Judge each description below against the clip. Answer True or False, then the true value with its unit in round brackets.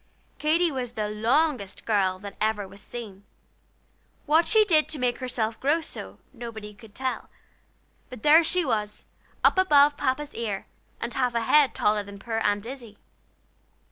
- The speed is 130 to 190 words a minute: True (160 wpm)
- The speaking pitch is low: False (235 Hz)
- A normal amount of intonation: False (5.7 semitones)